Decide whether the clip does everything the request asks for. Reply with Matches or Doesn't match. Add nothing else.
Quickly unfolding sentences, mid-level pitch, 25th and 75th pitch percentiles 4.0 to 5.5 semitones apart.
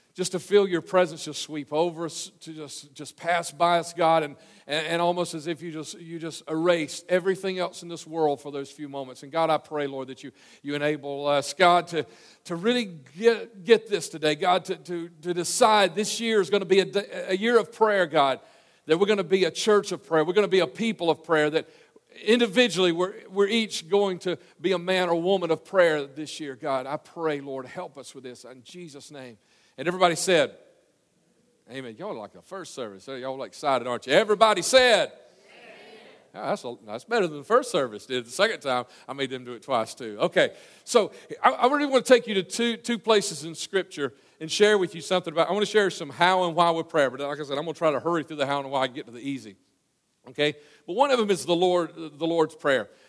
Matches